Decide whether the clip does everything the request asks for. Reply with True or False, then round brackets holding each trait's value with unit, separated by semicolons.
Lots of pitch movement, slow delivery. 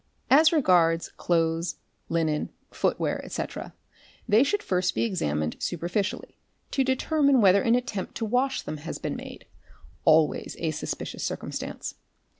True (7.2 semitones; 130 wpm)